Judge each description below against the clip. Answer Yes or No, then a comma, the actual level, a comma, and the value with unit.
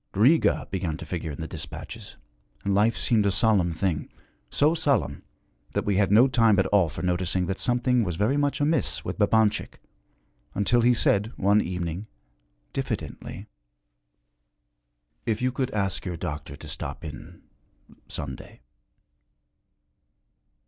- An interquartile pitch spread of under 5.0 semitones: No, wide, 5.4 semitones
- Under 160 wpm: Yes, average, 140 wpm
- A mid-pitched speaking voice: No, low, 100 Hz